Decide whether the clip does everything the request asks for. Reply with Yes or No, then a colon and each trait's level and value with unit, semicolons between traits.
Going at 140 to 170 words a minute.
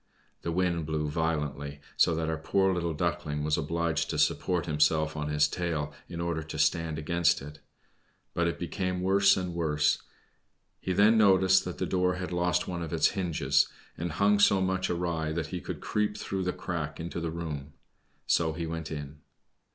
No: average, 185 wpm